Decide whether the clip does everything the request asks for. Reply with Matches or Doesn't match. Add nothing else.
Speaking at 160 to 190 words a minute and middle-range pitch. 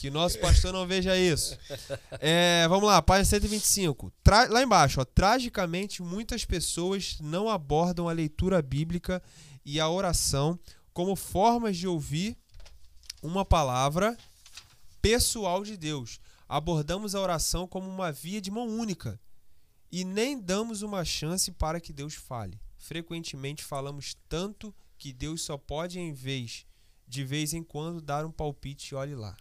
Doesn't match